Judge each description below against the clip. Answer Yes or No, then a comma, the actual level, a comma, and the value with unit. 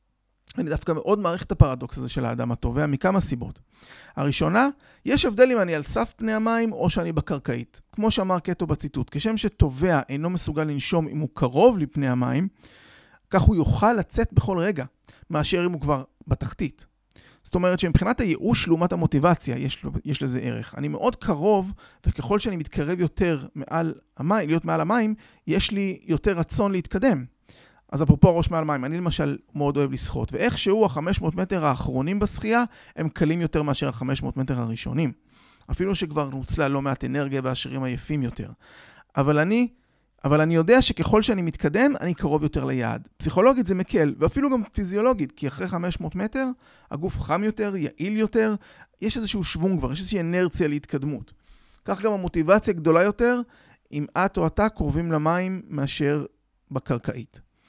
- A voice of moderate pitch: Yes, medium, 165 Hz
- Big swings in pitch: Yes, wide, 5.9 semitones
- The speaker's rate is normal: No, fast, 160 wpm